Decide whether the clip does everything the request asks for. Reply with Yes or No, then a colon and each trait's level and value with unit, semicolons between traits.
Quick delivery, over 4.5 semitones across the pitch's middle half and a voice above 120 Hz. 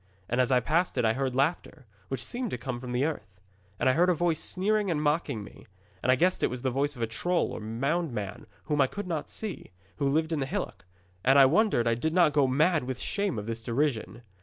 Yes: fast, 250 wpm; wide, 5.4 semitones; medium, 140 Hz